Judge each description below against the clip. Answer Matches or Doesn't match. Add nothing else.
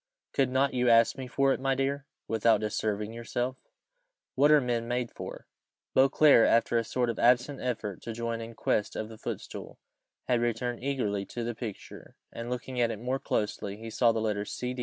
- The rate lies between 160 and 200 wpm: Matches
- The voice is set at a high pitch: Doesn't match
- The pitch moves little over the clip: Matches